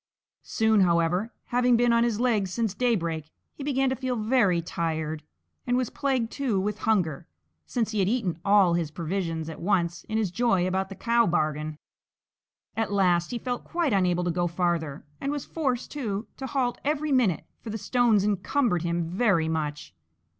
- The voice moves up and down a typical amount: No, wide, 6.0 semitones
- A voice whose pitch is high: Yes, high, 205 Hz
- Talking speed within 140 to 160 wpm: No, average, 180 wpm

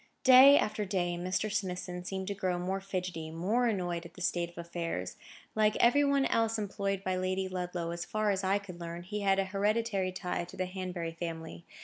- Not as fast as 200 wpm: No, fast, 205 wpm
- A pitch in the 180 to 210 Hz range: Yes, medium, 185 Hz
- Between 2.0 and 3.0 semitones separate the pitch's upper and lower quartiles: Yes, average, 2.7 semitones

